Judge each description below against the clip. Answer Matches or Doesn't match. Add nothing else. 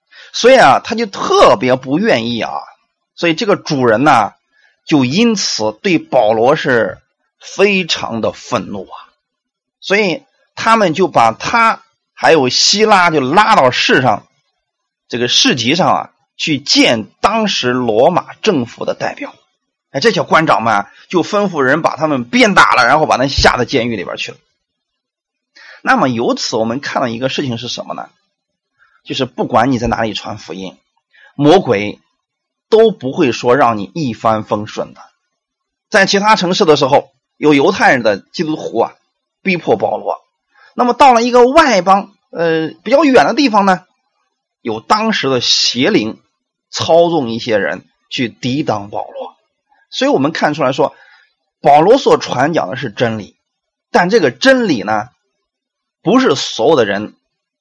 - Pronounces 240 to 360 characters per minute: Doesn't match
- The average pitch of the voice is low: Doesn't match